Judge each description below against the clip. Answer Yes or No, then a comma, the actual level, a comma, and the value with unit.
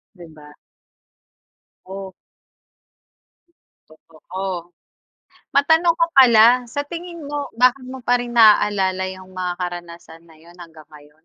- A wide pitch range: Yes, wide, 6.5 semitones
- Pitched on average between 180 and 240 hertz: Yes, high, 190 Hz